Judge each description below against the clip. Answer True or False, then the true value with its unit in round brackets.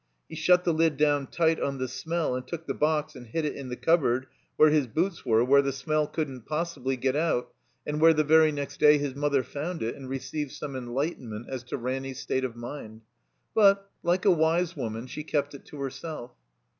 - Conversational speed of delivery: False (220 wpm)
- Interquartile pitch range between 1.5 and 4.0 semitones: True (3.6 semitones)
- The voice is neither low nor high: True (145 Hz)